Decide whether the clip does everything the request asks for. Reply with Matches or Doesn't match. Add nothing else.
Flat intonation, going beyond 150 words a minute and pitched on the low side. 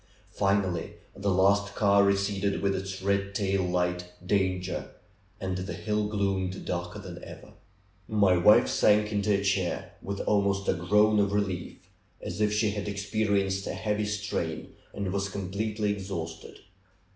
Doesn't match